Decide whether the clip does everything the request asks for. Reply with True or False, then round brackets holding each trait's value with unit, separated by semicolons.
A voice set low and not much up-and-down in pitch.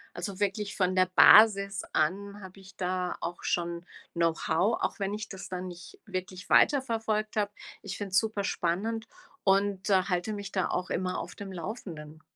False (195 Hz; 2.3 semitones)